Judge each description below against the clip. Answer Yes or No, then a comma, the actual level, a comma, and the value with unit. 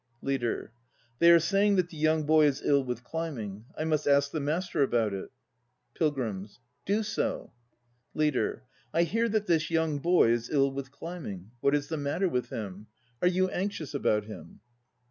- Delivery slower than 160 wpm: No, average, 175 wpm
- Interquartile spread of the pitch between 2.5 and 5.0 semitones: No, wide, 5.5 semitones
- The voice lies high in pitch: No, medium, 150 Hz